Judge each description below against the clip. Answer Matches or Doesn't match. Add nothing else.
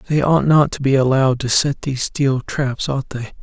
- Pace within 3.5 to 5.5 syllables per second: Matches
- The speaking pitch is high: Doesn't match